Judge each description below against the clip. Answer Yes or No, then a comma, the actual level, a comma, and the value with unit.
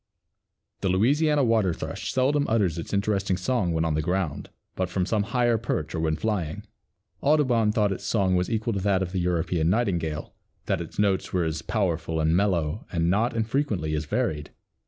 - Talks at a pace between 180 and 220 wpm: Yes, average, 185 wpm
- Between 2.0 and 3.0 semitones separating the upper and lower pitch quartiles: No, average, 5.0 semitones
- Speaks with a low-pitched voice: Yes, very low, 95 Hz